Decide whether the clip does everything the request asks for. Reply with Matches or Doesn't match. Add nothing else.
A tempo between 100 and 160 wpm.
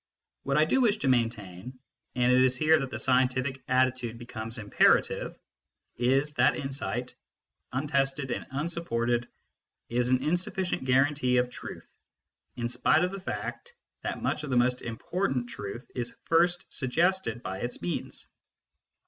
Matches